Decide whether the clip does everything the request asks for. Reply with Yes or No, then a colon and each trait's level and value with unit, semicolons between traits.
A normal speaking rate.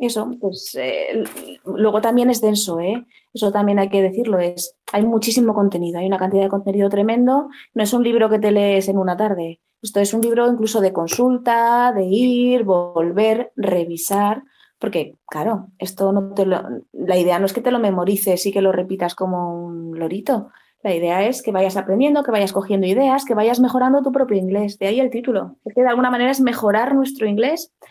No: fast, 200 wpm